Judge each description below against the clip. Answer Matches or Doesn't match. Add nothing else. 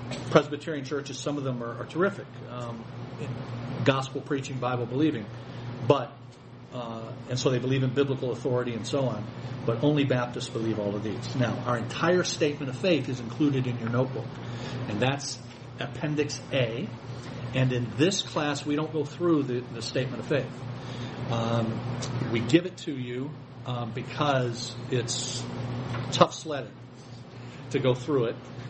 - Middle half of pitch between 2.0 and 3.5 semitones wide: Matches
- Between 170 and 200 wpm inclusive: Doesn't match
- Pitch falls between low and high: Doesn't match